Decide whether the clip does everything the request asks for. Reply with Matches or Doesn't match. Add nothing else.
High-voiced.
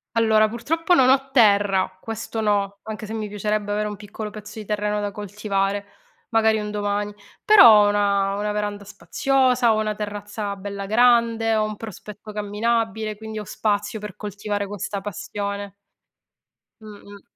Matches